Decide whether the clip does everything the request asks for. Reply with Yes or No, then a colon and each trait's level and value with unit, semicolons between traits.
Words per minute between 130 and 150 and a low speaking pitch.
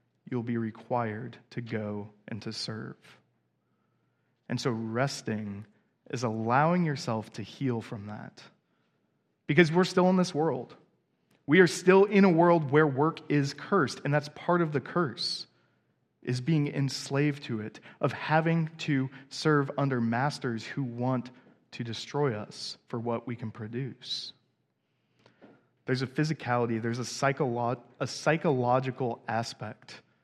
Yes: average, 140 wpm; low, 130 Hz